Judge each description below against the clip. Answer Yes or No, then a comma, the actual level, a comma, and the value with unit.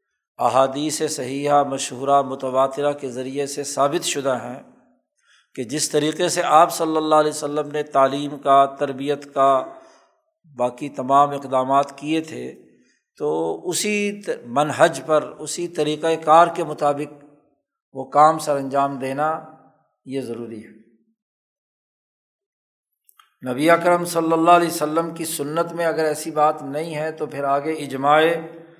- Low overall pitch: No, medium, 150 Hz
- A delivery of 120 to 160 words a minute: Yes, average, 140 wpm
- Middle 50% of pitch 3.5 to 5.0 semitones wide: No, average, 2.9 semitones